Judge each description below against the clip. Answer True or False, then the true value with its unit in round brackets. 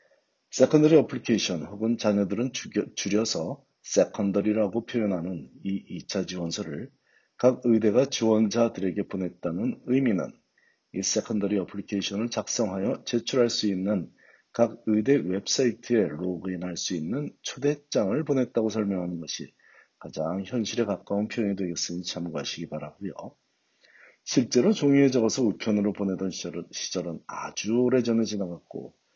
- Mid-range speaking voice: False (105 Hz)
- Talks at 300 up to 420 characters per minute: True (330 characters per minute)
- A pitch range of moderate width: True (3.8 semitones)